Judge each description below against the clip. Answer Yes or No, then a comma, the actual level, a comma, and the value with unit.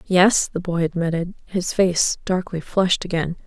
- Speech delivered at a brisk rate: No, average, 155 wpm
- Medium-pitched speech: Yes, medium, 175 Hz